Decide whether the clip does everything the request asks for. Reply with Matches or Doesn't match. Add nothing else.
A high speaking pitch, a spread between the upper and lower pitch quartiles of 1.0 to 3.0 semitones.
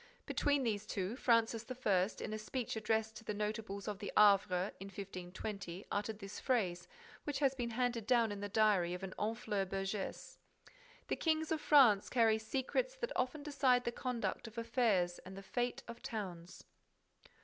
Doesn't match